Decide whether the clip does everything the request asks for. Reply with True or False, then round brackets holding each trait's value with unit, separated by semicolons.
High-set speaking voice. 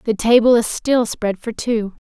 True (225 Hz)